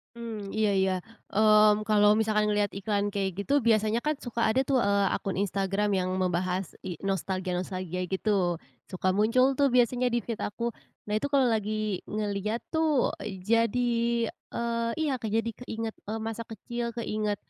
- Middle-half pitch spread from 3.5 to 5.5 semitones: No, average, 3.0 semitones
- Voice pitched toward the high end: Yes, high, 215 Hz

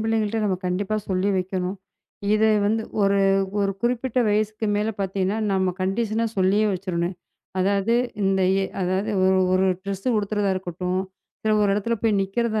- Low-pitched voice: No, high, 200 Hz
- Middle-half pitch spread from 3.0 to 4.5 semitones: No, narrow, 2.4 semitones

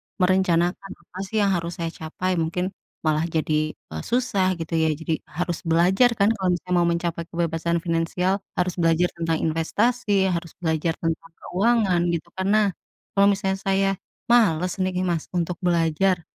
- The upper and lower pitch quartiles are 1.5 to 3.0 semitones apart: Yes, narrow, 2.6 semitones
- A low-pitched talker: No, medium, 175 Hz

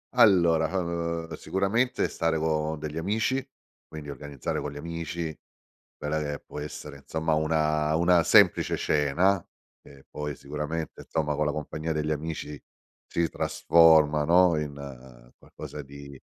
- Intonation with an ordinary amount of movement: No, narrow, 2.1 semitones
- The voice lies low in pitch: Yes, very low, 75 Hz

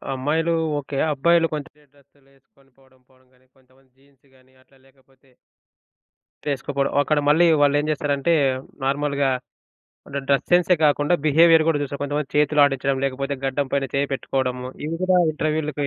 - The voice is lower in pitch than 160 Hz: Yes, medium, 140 Hz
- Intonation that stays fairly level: Yes, narrow, 1.7 semitones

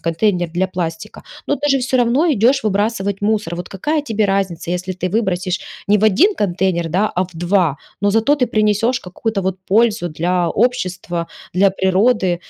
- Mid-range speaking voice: No, high, 195 Hz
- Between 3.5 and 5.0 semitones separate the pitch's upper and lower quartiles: Yes, average, 3.9 semitones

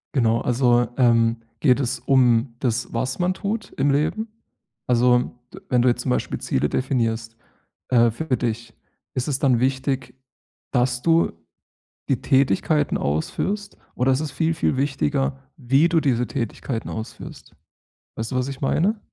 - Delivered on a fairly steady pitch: No, average, 3.0 semitones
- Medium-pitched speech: No, low, 130 Hz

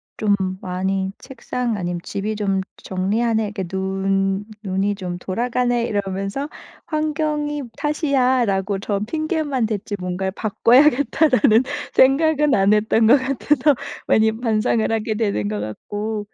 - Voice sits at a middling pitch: No, high, 215 Hz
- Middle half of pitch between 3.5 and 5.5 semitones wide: Yes, average, 5.1 semitones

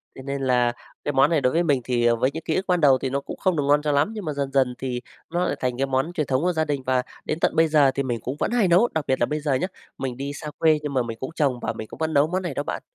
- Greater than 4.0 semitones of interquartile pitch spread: No, average, 3.3 semitones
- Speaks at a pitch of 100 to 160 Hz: Yes, medium, 140 Hz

